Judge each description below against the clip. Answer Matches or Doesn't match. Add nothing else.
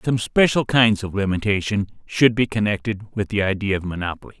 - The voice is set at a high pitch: Doesn't match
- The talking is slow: Doesn't match